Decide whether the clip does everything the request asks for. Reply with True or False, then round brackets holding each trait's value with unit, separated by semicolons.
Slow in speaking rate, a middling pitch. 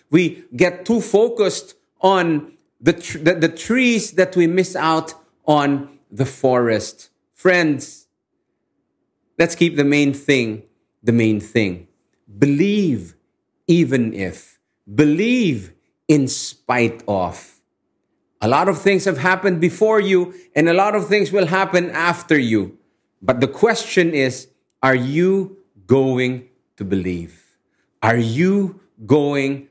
True (125 wpm; 160 Hz)